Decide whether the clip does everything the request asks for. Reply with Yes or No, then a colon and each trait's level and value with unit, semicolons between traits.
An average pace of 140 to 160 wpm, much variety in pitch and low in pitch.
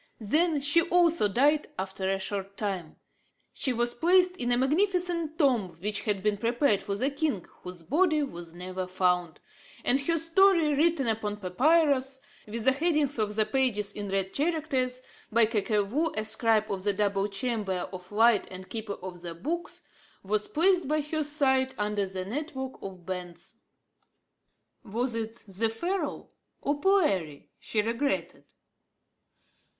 No: average, 150 wpm; wide, 7.1 semitones; high, 230 Hz